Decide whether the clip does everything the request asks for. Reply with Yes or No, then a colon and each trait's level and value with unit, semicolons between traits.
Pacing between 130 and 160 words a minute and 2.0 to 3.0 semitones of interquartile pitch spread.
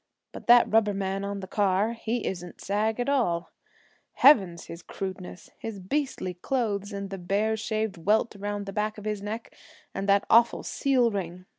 No: average, 175 wpm; narrow, 2.5 semitones